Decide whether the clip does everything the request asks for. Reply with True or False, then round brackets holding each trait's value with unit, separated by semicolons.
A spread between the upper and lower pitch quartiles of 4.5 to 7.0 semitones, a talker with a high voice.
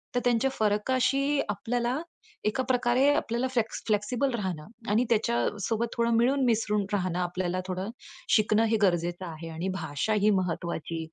True (4.8 semitones; 215 Hz)